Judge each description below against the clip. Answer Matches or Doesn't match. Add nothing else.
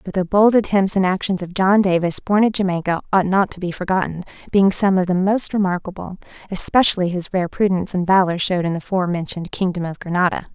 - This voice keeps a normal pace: Doesn't match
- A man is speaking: Doesn't match